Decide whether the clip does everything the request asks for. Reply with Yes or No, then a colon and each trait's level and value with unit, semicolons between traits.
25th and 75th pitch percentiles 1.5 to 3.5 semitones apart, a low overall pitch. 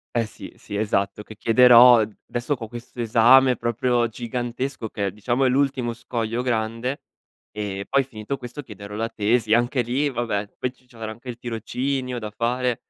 Yes: narrow, 2.4 semitones; low, 120 Hz